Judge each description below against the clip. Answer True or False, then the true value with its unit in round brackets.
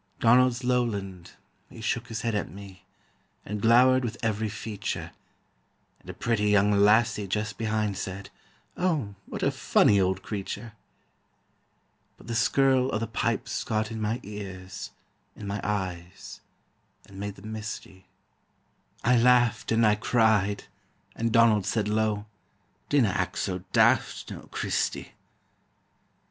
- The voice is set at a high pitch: False (110 Hz)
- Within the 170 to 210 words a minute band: False (135 wpm)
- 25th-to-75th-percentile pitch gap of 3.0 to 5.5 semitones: False (2.4 semitones)